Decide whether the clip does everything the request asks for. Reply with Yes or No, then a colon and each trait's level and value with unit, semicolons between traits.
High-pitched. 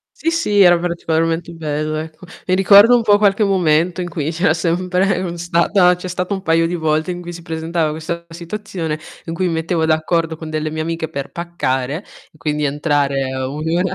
No: medium, 165 Hz